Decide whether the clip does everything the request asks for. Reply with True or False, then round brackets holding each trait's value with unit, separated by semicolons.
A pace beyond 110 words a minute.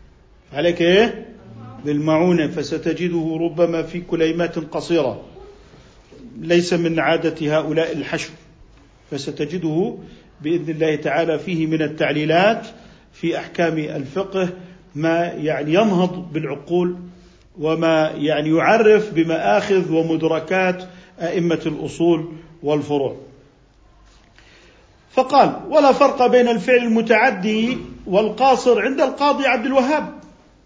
False (90 wpm)